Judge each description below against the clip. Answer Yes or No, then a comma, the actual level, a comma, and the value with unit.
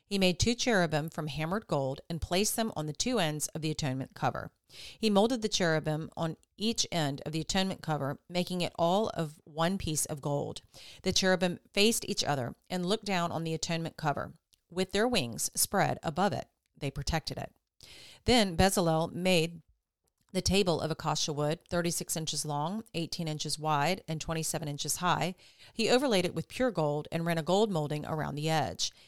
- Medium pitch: Yes, medium, 165 Hz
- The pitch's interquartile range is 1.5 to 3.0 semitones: No, average, 3.5 semitones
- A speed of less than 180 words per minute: No, average, 185 wpm